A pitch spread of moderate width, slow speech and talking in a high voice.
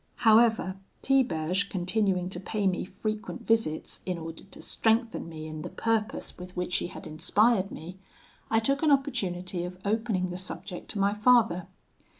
No: average, 3.9 semitones; average, 160 wpm; high, 195 Hz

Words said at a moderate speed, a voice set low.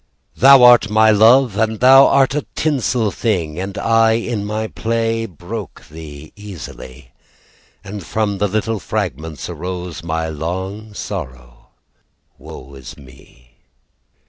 No: slow, 125 wpm; low, 105 Hz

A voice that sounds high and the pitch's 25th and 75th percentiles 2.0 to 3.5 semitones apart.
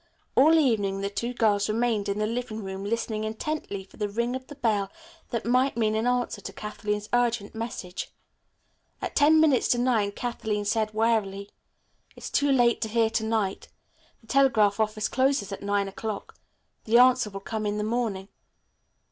Yes: high, 220 Hz; average, 2.9 semitones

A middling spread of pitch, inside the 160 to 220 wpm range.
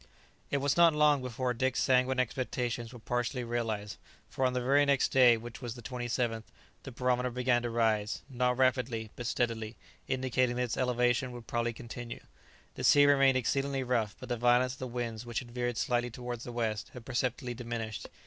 No: narrow, 1.5 semitones; average, 190 wpm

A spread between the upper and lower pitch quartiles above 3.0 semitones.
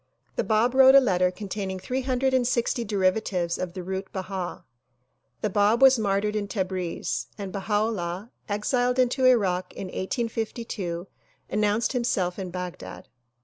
Yes: average, 4.2 semitones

